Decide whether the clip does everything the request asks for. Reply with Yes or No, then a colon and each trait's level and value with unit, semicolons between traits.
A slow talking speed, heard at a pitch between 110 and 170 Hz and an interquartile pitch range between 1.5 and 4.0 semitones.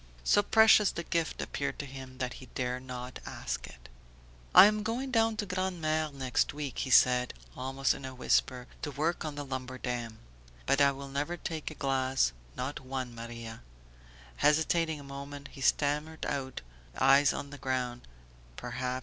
No: average, 170 wpm; low, 135 Hz; average, 3.4 semitones